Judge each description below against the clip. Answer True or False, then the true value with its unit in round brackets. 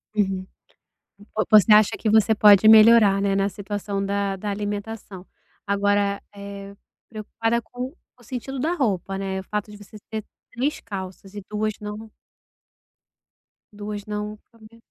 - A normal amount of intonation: False (1.6 semitones)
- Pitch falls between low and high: False (210 Hz)